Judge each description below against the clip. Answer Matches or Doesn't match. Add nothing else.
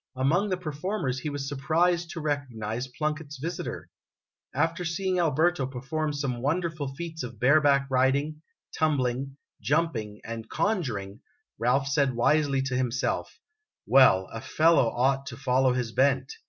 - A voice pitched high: Doesn't match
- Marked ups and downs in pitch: Doesn't match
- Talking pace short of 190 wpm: Matches